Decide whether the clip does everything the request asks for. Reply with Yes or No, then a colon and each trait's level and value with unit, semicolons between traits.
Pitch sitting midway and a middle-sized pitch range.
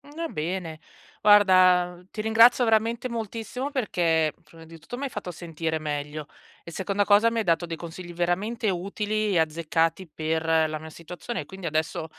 Yes: medium, 180 Hz; average, 4.8 semitones